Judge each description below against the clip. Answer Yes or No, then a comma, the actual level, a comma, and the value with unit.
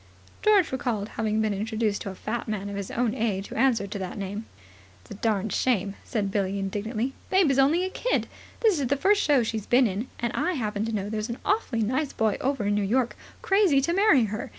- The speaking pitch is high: Yes, high, 225 Hz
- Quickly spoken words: Yes, fast, 230 wpm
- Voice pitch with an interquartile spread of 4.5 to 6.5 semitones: Yes, average, 4.8 semitones